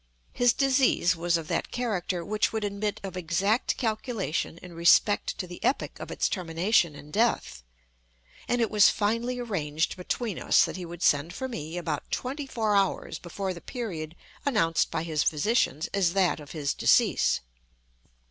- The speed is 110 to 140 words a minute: No, average, 165 wpm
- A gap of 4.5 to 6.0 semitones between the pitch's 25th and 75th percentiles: Yes, average, 5.1 semitones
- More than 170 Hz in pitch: Yes, medium, 185 Hz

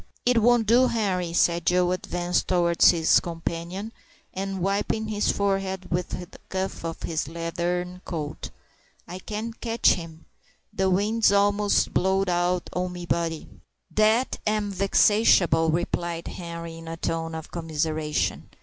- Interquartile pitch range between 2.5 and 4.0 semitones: Yes, average, 3.2 semitones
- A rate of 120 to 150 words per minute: Yes, average, 140 wpm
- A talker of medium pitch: Yes, medium, 180 Hz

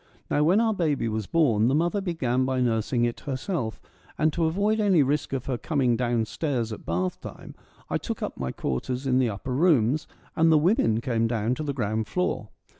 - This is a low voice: Yes, low, 130 Hz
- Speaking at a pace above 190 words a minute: Yes, fast, 205 wpm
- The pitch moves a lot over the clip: Yes, wide, 5.8 semitones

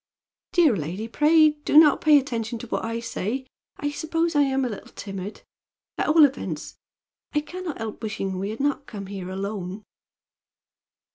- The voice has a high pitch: Yes, high, 235 Hz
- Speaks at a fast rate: No, average, 180 wpm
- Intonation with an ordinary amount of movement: No, wide, 6.6 semitones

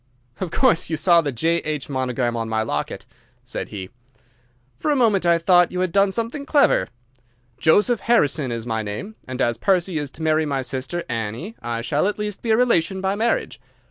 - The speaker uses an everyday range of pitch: No, wide, 7.8 semitones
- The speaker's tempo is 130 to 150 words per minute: No, average, 195 wpm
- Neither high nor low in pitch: Yes, medium, 165 Hz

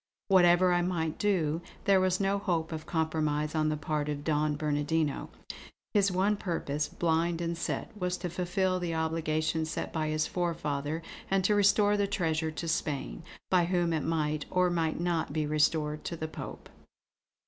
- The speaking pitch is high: No, medium, 165 Hz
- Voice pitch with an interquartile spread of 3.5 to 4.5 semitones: No, average, 2.8 semitones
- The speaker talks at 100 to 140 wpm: No, average, 170 wpm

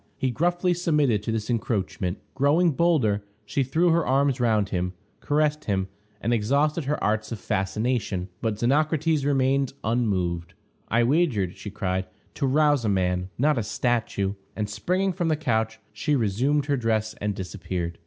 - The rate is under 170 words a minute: Yes, average, 160 wpm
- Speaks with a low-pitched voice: Yes, low, 120 Hz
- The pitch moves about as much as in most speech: No, wide, 6.1 semitones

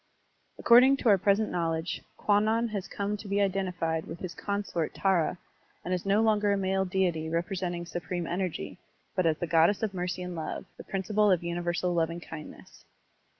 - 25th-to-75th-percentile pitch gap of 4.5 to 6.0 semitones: No, average, 2.8 semitones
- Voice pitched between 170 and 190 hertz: Yes, medium, 185 Hz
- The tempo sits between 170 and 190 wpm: Yes, average, 175 wpm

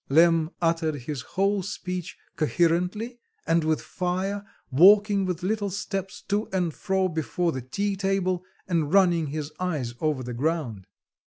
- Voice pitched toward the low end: No, medium, 175 Hz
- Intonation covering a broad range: No, average, 3.7 semitones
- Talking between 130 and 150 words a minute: Yes, average, 145 wpm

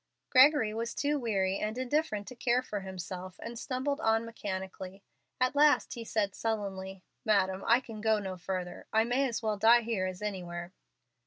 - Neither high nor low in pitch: No, high, 215 Hz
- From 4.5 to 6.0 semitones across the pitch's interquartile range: No, average, 4.0 semitones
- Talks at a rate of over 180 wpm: No, average, 175 wpm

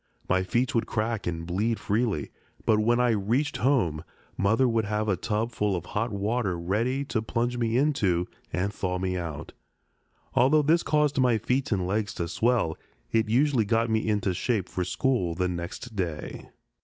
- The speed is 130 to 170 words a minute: No, average, 180 wpm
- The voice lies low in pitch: Yes, low, 110 Hz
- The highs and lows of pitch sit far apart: No, average, 4.7 semitones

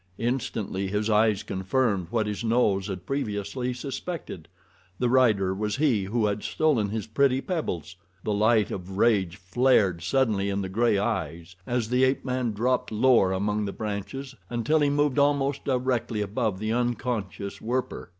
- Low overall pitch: Yes, low, 110 Hz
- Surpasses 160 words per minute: No, average, 155 wpm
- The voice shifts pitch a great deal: No, average, 4.4 semitones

